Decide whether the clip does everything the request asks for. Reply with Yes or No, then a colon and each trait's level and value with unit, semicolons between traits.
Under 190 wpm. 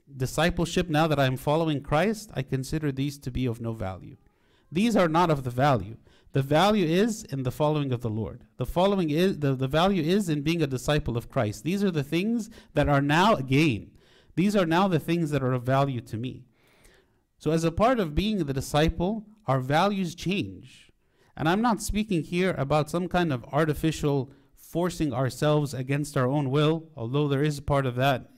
No: average, 200 wpm